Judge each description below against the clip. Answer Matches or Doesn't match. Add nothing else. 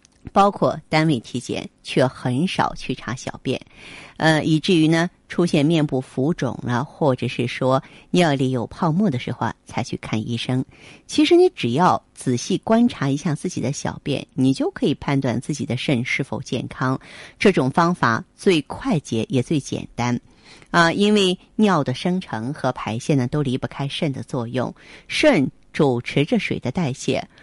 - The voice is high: Doesn't match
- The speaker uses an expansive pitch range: Doesn't match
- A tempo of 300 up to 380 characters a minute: Doesn't match